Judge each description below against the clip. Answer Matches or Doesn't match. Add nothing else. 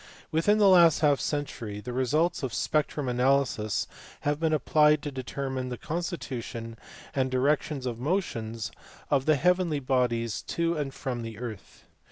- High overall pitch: Doesn't match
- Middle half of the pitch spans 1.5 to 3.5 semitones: Doesn't match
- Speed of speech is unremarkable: Matches